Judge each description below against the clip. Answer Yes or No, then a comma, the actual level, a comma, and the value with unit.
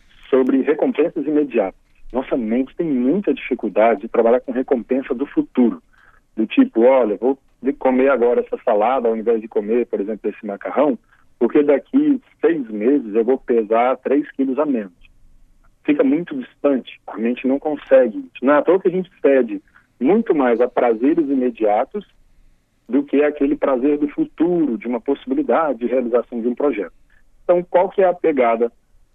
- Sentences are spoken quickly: No, average, 160 wpm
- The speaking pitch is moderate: Yes, medium, 145 Hz